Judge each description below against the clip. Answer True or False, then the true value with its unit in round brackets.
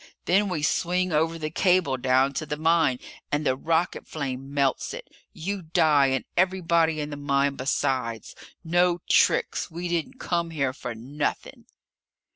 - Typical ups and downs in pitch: True (3.8 semitones)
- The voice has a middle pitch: True (155 Hz)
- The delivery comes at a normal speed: True (155 wpm)